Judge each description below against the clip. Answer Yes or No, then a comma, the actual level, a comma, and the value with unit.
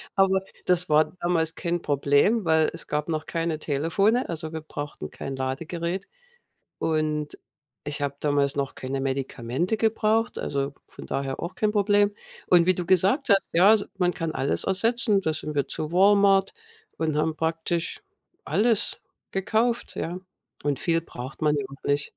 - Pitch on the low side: No, medium, 165 Hz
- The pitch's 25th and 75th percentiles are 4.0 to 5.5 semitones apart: Yes, average, 4.8 semitones